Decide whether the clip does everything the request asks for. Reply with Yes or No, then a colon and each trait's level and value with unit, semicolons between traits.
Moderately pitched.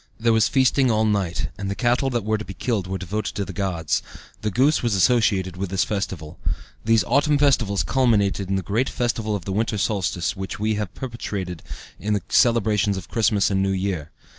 No: low, 105 Hz